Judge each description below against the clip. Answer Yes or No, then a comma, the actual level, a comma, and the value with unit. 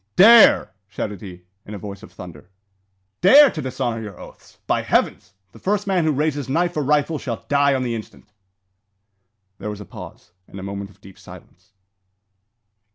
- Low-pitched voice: Yes, low, 120 Hz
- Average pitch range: No, wide, 7.5 semitones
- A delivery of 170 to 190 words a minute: Yes, average, 175 wpm